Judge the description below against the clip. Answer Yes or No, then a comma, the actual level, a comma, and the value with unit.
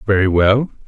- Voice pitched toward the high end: No, low, 105 Hz